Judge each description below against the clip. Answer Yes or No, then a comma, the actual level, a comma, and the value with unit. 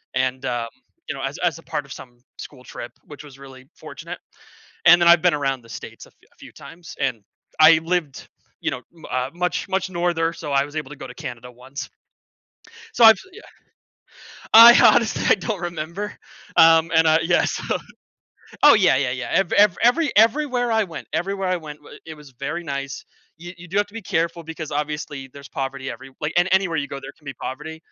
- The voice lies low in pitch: No, medium, 160 Hz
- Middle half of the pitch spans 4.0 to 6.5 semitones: Yes, average, 4.5 semitones